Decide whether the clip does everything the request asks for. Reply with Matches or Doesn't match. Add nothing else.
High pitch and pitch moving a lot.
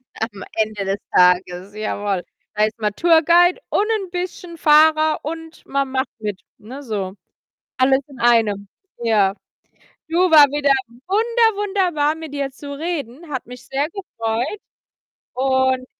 Matches